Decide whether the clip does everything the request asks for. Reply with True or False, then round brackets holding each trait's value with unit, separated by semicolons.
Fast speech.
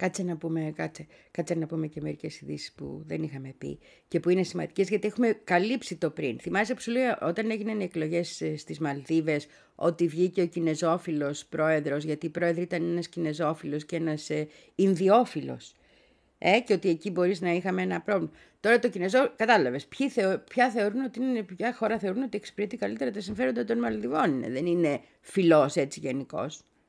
True (175 wpm)